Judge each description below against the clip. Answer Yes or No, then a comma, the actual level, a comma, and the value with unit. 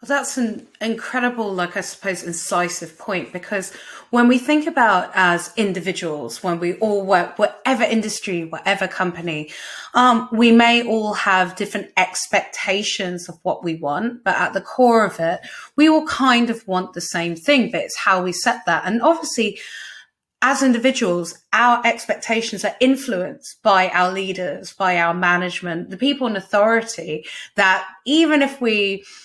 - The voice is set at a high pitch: Yes, high, 200 Hz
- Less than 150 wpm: No, average, 160 wpm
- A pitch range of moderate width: Yes, average, 4.8 semitones